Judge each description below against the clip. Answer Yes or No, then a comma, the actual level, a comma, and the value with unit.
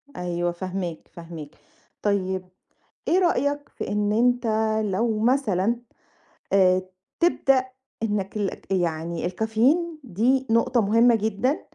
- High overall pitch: Yes, high, 210 Hz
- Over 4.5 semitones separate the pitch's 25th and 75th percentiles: Yes, average, 5.1 semitones